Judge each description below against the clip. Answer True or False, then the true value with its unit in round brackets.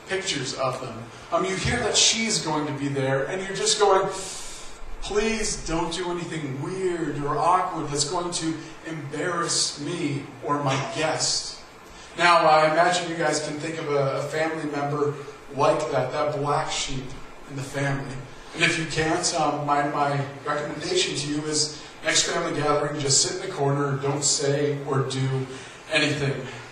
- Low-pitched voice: False (150 Hz)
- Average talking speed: True (170 wpm)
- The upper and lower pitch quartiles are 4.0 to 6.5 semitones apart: False (3.2 semitones)